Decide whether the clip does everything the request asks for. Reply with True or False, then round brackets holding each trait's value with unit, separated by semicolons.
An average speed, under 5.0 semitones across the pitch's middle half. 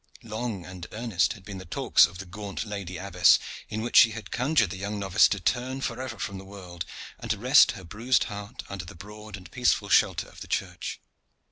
False (215 wpm; 3.1 semitones)